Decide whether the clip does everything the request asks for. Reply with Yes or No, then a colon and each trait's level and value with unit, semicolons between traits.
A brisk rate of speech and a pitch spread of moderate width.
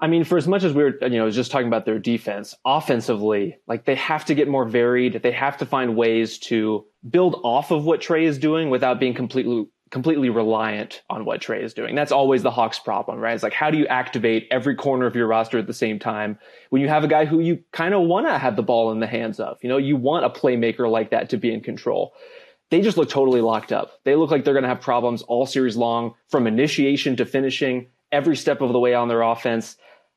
Yes: fast, 250 wpm; average, 4.3 semitones